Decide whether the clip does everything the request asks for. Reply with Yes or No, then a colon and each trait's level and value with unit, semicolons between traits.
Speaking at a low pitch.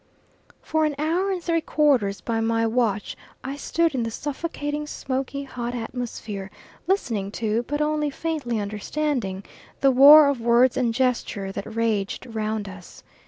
No: very high, 250 Hz